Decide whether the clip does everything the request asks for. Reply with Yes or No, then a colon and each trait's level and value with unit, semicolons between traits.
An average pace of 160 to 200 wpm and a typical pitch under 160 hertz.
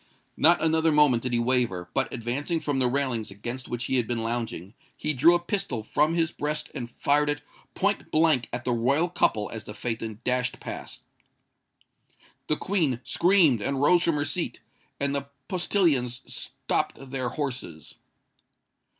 Yes: average, 165 wpm; low, 135 Hz